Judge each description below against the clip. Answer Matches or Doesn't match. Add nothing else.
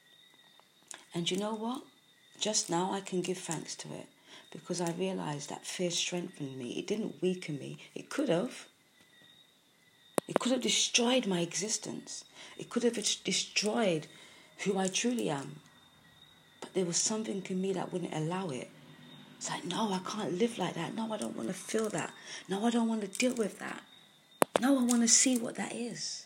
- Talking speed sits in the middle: Matches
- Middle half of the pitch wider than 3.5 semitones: Matches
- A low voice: Doesn't match